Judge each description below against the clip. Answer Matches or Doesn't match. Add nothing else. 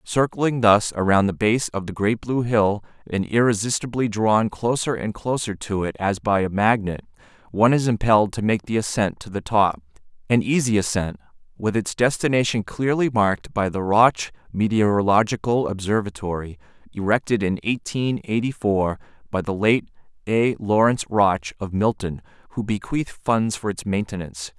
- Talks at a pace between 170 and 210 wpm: Doesn't match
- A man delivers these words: Matches